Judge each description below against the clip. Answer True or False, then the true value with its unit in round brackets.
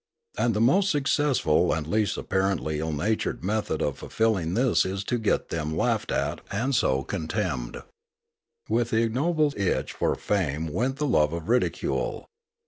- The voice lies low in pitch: True (105 Hz)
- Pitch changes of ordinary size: False (7.2 semitones)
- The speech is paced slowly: False (160 wpm)